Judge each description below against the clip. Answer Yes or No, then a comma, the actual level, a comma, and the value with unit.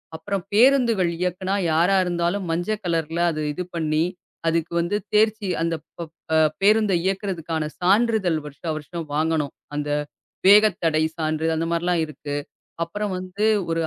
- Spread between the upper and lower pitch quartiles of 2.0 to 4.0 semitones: Yes, average, 3.6 semitones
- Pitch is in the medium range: Yes, medium, 175 Hz